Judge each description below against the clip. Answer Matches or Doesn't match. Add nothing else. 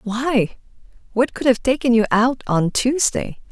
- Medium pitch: Doesn't match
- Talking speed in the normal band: Matches